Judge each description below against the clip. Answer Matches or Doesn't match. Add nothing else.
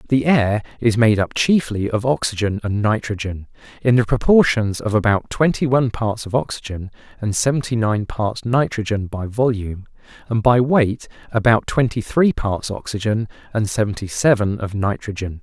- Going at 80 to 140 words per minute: Doesn't match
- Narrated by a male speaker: Matches